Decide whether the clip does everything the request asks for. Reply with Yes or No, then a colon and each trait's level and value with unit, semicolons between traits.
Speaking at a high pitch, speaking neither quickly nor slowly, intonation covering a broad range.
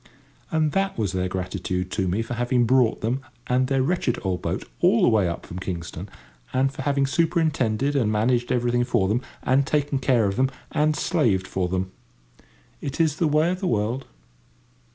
No: low, 125 Hz; average, 190 wpm; wide, 5.7 semitones